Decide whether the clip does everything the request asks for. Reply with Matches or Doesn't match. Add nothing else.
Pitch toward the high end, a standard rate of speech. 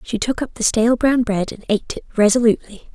Doesn't match